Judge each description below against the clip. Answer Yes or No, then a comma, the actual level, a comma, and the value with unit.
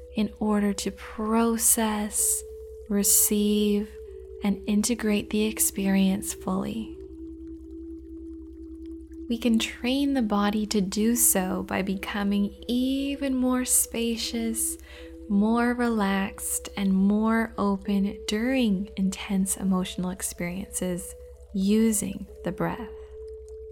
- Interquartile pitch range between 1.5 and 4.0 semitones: No, wide, 5.6 semitones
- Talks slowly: Yes, slow, 90 wpm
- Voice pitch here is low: No, high, 215 Hz